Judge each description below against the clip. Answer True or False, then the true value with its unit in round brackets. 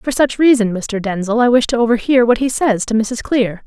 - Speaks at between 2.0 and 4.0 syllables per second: False (5.2 syllables/s)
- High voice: True (230 Hz)